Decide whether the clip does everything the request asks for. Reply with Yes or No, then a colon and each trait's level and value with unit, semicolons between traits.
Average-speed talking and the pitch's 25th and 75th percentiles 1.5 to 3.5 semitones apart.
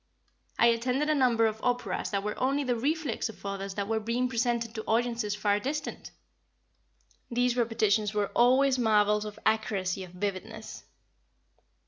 Yes: average, 150 wpm; average, 3.0 semitones